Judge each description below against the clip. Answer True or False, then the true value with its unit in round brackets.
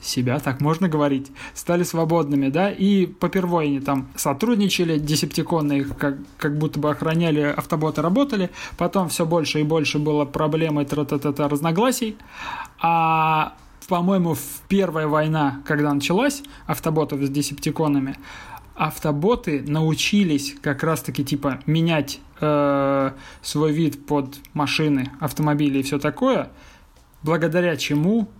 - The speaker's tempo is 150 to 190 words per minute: False (120 wpm)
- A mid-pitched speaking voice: True (155 Hz)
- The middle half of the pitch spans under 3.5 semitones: True (2.6 semitones)